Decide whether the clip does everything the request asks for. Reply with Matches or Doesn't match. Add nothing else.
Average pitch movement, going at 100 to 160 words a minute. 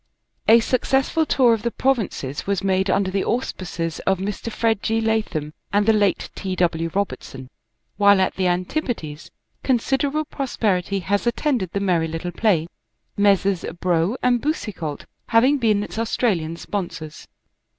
Matches